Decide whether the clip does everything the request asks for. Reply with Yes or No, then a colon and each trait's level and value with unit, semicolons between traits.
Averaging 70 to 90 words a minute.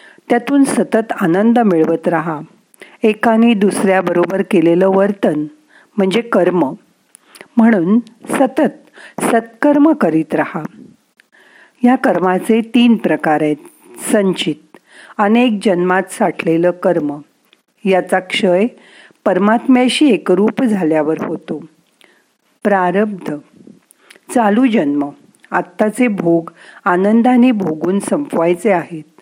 Yes: average, 85 wpm